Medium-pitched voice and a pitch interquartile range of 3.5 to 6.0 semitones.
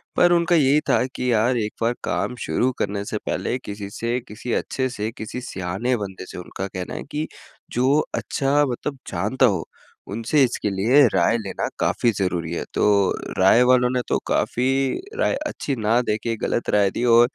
No: low, 115 Hz; average, 4.0 semitones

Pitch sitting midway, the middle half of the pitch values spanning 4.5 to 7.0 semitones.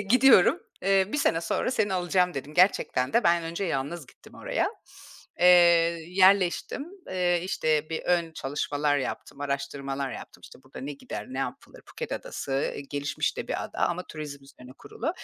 Yes: medium, 165 Hz; average, 4.8 semitones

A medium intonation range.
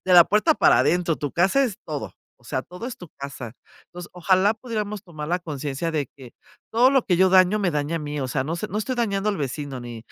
No: wide, 5.9 semitones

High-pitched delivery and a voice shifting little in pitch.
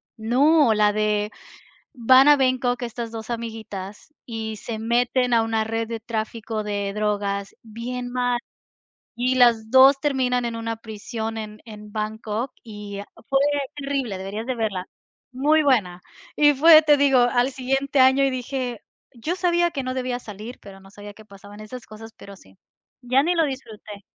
No: high, 230 Hz; average, 3.3 semitones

